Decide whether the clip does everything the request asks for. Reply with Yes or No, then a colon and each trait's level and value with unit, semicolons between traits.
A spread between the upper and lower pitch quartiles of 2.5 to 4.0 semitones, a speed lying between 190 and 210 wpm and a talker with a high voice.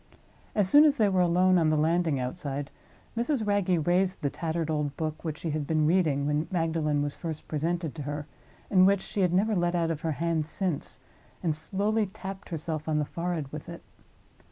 No: average, 3.4 semitones; fast, 205 wpm; medium, 165 Hz